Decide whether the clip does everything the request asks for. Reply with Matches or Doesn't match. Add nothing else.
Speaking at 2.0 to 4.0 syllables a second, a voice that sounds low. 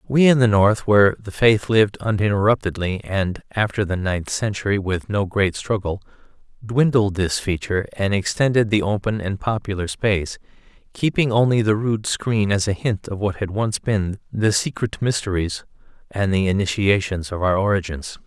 Doesn't match